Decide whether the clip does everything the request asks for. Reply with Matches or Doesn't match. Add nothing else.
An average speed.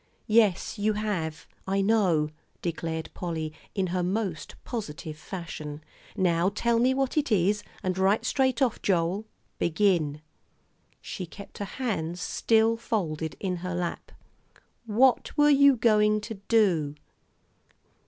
Doesn't match